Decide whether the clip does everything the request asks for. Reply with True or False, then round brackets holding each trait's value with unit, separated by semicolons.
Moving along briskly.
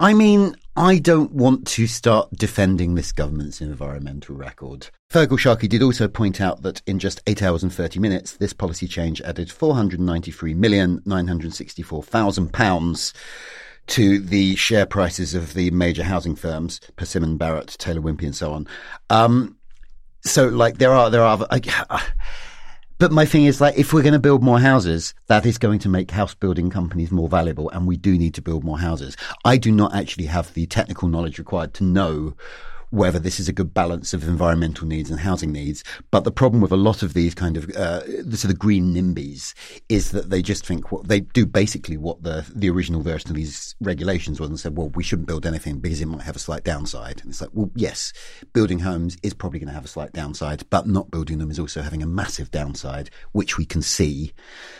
True (210 wpm)